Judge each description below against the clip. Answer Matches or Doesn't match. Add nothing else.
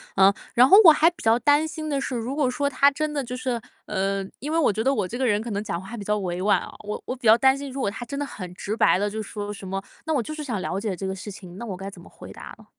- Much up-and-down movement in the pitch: Matches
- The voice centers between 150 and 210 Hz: Doesn't match